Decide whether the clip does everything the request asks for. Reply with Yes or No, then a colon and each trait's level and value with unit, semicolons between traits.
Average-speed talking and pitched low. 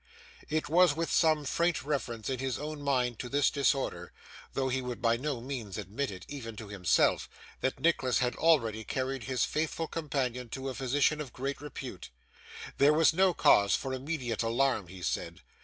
Yes: average, 180 wpm; low, 130 Hz